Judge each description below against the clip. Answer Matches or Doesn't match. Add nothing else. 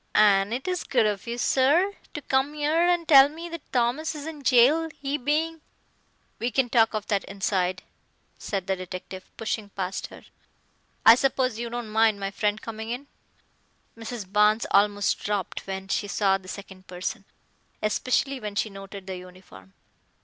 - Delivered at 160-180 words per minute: Matches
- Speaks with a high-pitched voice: Matches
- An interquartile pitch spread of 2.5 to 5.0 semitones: Doesn't match